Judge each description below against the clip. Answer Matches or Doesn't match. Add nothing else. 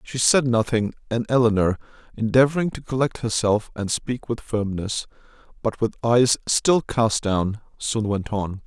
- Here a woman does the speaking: Doesn't match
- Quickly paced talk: Doesn't match